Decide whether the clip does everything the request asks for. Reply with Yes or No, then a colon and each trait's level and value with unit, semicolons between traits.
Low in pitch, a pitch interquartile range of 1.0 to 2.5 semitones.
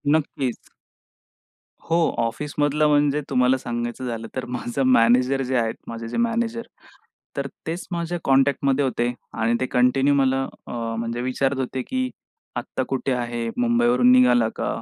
No: low, 130 Hz; average, 2.9 semitones